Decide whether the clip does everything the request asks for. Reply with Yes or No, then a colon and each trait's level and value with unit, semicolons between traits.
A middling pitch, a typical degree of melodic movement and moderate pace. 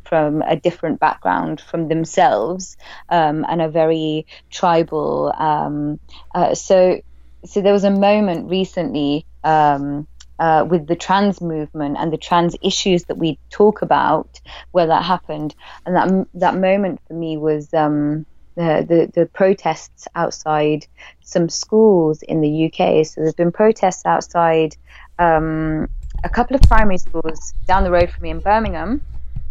Yes: medium, 165 Hz; average, 3.0 semitones; average, 150 wpm